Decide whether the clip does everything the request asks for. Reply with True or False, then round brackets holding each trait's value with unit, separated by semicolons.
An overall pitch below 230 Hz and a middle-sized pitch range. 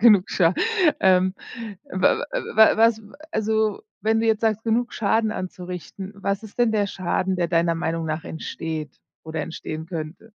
True (190 Hz; 4.6 semitones)